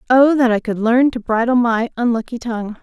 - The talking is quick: Yes, fast, 210 wpm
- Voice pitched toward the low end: No, high, 235 Hz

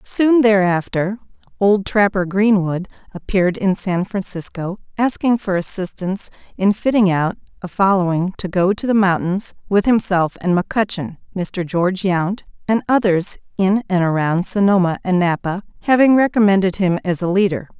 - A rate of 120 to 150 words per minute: Yes, average, 140 wpm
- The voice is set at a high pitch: Yes, high, 195 Hz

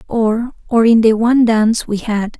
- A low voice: No, high, 225 Hz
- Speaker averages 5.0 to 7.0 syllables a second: No, 4.8 syllables/s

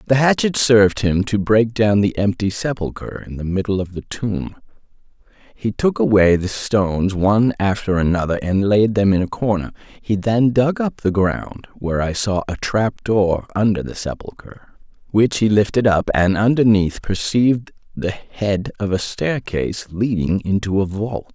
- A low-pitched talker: Yes, low, 105 Hz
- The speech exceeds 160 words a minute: Yes, average, 170 wpm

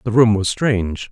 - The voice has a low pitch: Yes, low, 105 Hz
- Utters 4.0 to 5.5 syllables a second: Yes, 5.1 syllables/s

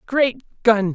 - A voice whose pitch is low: No, high, 225 Hz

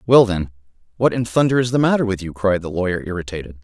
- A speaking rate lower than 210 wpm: No, fast, 230 wpm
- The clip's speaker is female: No, male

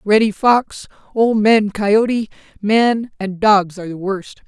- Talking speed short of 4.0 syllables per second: Yes, 3.8 syllables/s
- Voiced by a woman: Yes, female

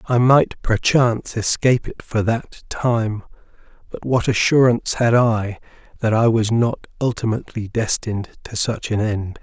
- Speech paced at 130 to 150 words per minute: Yes, average, 145 wpm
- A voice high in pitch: No, low, 115 Hz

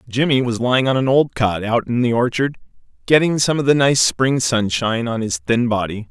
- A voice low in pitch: Yes, low, 120 Hz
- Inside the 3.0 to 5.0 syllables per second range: No, 5.3 syllables/s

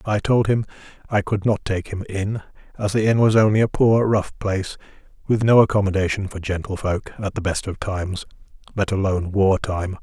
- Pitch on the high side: No, low, 100 Hz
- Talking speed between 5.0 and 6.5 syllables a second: Yes, 5.5 syllables/s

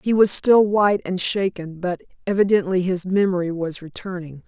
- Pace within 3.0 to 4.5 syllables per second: No, 5.1 syllables/s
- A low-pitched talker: No, medium, 185 Hz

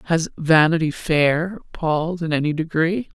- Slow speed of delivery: Yes, slow, 130 wpm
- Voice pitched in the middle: Yes, medium, 160 Hz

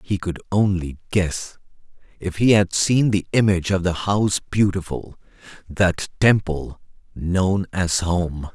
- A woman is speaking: No, male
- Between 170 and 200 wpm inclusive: No, slow, 135 wpm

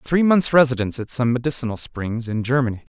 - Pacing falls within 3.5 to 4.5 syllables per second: No, 6.5 syllables/s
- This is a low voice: Yes, low, 125 Hz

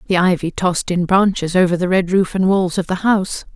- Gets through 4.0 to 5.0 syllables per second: No, 5.8 syllables/s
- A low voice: No, medium, 185 Hz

